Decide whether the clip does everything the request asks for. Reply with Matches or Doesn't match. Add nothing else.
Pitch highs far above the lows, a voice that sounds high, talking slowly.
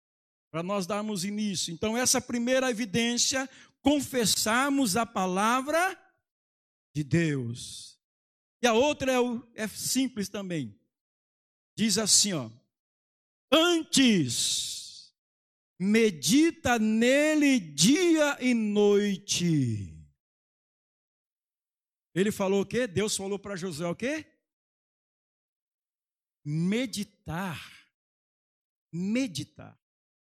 Matches